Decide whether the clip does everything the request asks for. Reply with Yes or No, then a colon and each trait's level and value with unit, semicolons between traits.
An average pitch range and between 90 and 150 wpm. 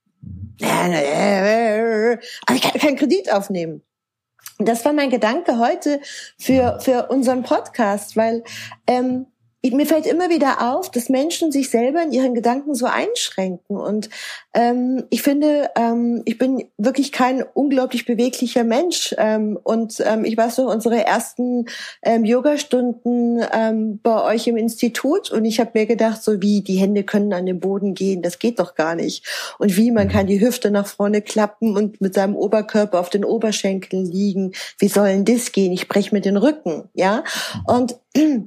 No: average, 3.9 semitones; average, 165 wpm